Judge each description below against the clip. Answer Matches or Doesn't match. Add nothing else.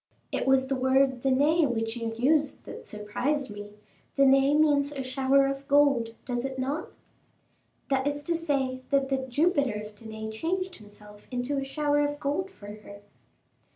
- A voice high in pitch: Matches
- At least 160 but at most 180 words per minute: Matches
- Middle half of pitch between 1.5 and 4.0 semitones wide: Matches